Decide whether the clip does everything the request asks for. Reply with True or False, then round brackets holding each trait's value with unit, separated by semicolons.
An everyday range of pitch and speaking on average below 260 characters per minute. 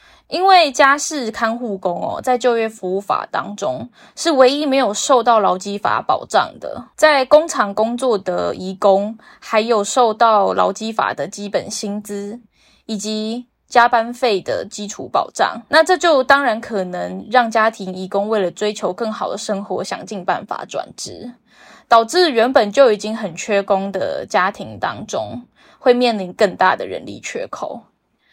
True (4.0 semitones; 235 characters per minute)